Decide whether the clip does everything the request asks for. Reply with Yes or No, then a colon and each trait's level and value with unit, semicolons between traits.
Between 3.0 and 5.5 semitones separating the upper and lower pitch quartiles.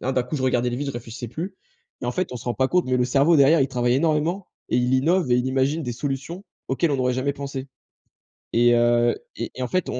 Yes: average, 3.5 semitones